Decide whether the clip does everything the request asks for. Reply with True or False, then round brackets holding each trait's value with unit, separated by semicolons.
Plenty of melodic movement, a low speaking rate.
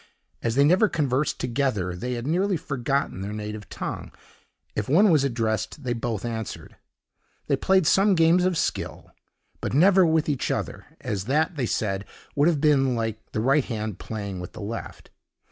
False (6.2 semitones; 175 wpm)